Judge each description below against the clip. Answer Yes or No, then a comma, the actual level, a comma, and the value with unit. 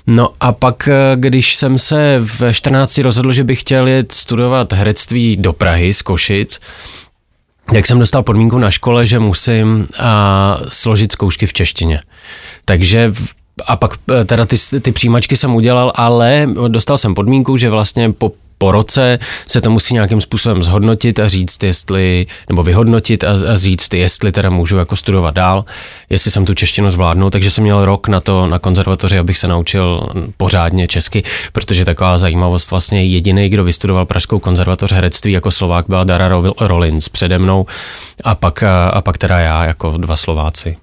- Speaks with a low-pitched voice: Yes, low, 100 Hz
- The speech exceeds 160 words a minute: Yes, fast, 170 wpm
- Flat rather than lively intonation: No, average, 4.2 semitones